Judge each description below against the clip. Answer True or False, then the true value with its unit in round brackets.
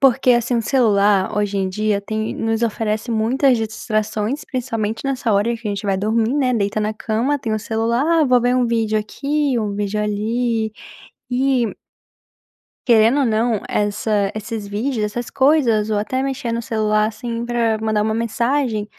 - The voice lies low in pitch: False (225 Hz)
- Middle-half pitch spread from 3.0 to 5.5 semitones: False (2.5 semitones)